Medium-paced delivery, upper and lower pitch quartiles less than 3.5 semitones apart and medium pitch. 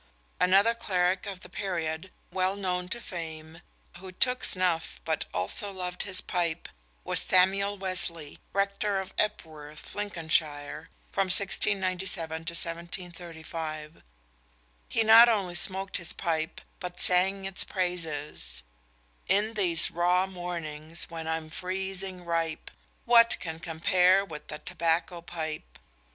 No: slow, 120 wpm; average, 2.9 semitones; medium, 180 Hz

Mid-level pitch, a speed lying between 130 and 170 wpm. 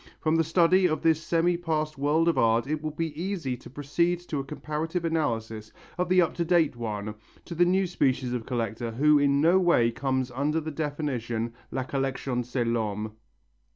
No: medium, 150 Hz; average, 190 wpm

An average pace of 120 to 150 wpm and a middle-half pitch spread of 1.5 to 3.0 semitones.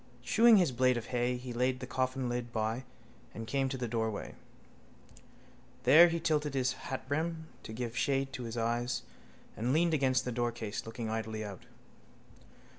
No: average, 160 wpm; narrow, 2.6 semitones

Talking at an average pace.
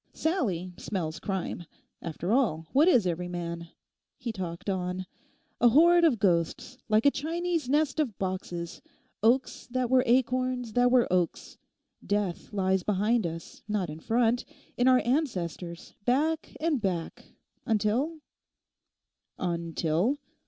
No: slow, 120 wpm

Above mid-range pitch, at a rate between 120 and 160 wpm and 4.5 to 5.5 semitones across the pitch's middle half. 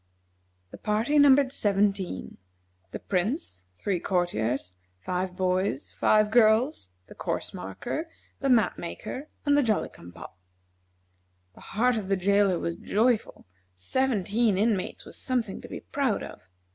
Yes: high, 205 Hz; slow, 135 wpm; average, 5.2 semitones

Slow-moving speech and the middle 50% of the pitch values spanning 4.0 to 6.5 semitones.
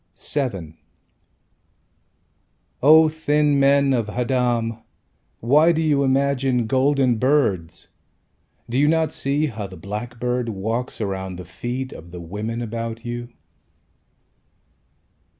Yes: slow, 110 wpm; average, 4.3 semitones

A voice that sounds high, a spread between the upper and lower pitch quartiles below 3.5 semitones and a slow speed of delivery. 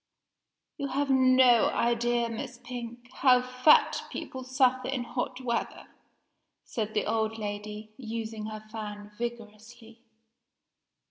Yes: high, 235 Hz; narrow, 2.5 semitones; slow, 115 wpm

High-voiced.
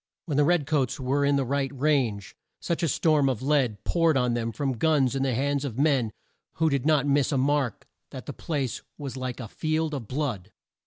No: medium, 140 Hz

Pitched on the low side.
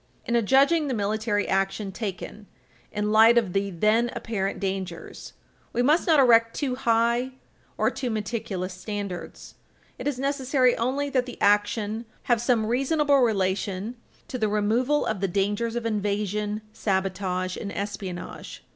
No: high, 215 Hz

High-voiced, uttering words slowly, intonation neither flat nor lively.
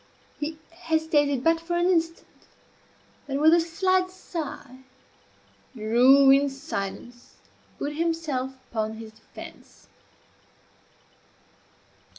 Yes: very high, 295 Hz; slow, 100 wpm; average, 4.4 semitones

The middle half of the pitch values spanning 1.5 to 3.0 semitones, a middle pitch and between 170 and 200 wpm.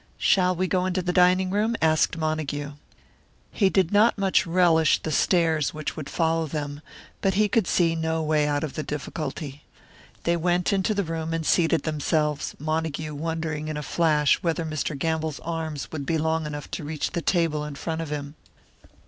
Yes: narrow, 2.4 semitones; medium, 160 Hz; average, 190 wpm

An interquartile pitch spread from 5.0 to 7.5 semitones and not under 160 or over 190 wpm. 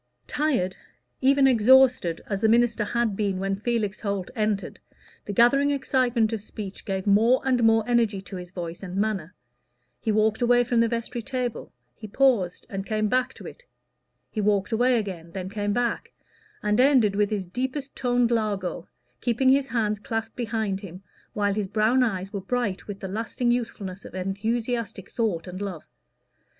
No: average, 3.6 semitones; average, 170 wpm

